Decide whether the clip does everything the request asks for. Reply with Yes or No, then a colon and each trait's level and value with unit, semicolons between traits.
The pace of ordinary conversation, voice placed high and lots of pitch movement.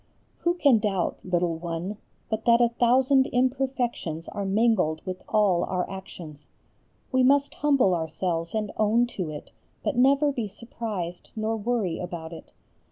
Yes: average, 150 wpm; high, 210 Hz; wide, 5.7 semitones